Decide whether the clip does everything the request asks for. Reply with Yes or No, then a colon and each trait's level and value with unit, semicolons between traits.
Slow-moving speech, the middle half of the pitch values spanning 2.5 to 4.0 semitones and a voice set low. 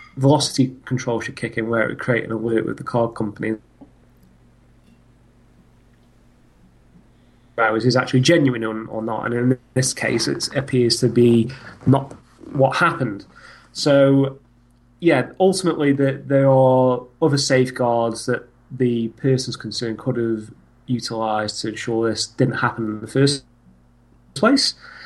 Yes: slow, 130 wpm; average, 3.0 semitones; low, 120 Hz